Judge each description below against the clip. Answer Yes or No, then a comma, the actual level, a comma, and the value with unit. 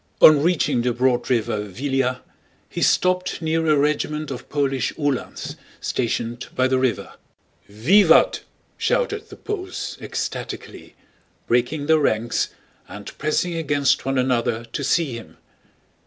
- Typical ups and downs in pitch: Yes, average, 4.5 semitones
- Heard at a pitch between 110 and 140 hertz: Yes, low, 135 Hz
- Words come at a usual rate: No, slow, 125 wpm